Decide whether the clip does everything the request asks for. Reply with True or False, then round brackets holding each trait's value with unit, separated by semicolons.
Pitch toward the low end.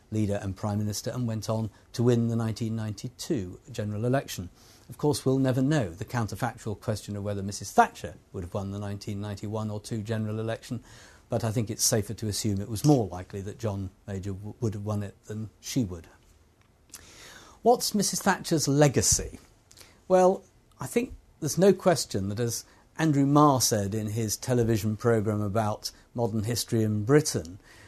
True (110 Hz)